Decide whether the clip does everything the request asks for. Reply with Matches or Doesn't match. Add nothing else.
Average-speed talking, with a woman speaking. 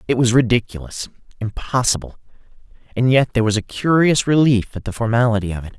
Doesn't match